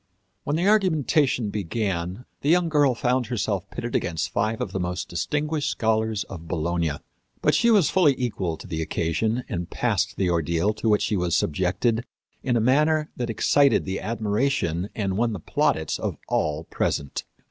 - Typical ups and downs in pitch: No, wide, 6.6 semitones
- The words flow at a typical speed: Yes, average, 170 wpm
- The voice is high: No, low, 110 Hz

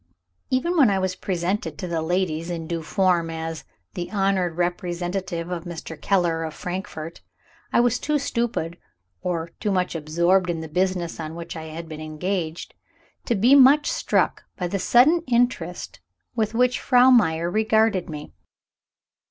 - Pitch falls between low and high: Yes, medium, 180 Hz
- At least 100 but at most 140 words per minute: No, average, 160 wpm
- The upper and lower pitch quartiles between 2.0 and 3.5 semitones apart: No, average, 4.5 semitones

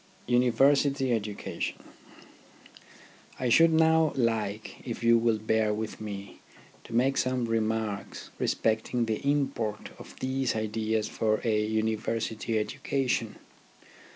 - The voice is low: Yes, low, 115 Hz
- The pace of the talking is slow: Yes, slow, 110 wpm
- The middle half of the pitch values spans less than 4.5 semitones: Yes, average, 2.8 semitones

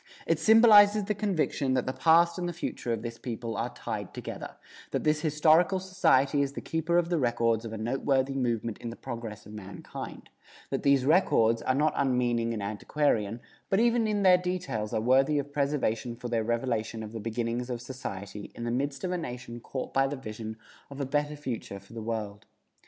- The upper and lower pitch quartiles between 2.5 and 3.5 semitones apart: No, average, 5.1 semitones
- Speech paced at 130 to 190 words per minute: No, average, 200 wpm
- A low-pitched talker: Yes, low, 130 Hz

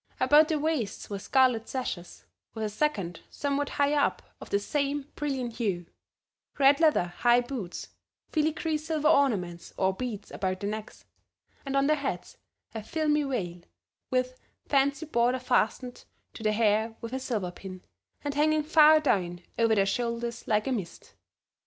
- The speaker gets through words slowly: No, average, 160 wpm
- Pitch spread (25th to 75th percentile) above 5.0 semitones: Yes, wide, 5.5 semitones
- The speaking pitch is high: Yes, very high, 250 Hz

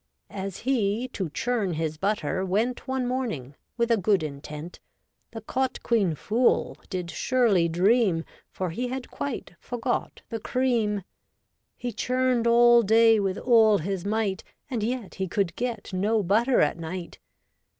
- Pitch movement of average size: Yes, average, 4.5 semitones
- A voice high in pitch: Yes, high, 215 Hz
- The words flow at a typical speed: Yes, average, 150 wpm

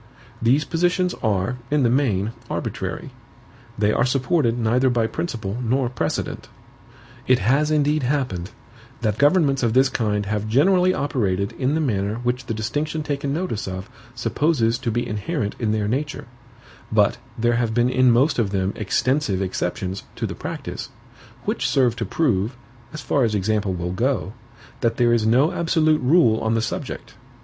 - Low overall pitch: Yes, low, 120 Hz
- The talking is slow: No, average, 165 wpm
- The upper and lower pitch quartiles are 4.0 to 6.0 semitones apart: Yes, average, 4.9 semitones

